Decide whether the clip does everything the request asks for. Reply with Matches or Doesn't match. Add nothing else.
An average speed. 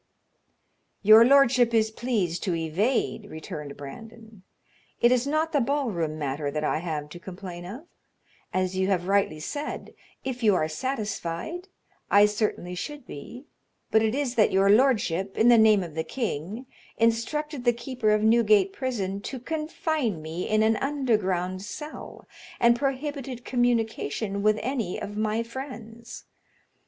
Matches